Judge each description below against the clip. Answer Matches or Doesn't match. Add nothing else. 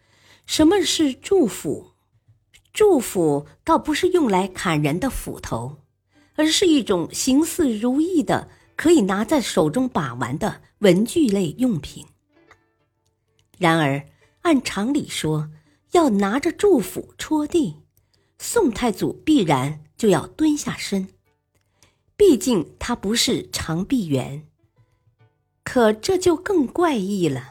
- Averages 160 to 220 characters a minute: Matches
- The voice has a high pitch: Matches